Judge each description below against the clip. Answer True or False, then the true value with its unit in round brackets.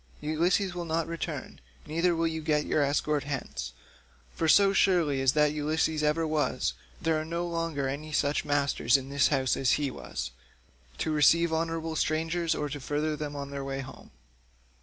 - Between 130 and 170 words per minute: False (180 wpm)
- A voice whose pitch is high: False (150 Hz)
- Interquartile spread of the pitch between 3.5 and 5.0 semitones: False (2.5 semitones)